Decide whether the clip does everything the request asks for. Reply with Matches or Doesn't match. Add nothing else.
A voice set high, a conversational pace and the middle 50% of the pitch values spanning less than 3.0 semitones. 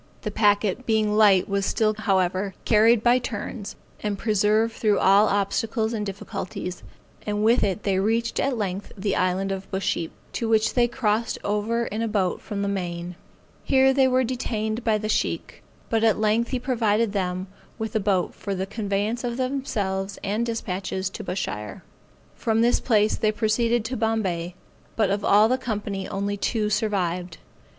Matches